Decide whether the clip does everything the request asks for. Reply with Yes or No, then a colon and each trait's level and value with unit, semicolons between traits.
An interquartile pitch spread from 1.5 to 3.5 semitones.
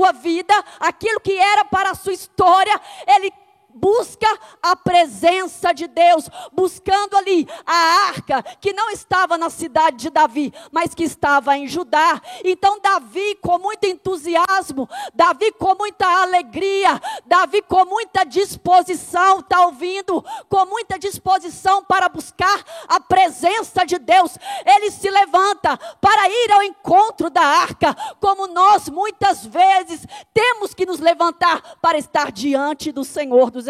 Yes: average, 2.7 semitones